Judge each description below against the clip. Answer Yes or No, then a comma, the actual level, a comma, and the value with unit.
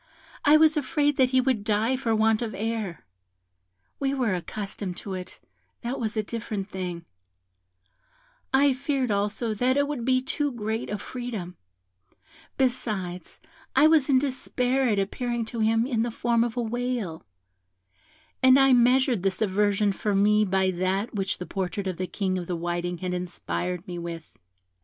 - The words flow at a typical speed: Yes, average, 165 wpm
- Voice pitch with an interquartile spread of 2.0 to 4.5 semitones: No, average, 5.0 semitones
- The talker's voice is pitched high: Yes, high, 220 Hz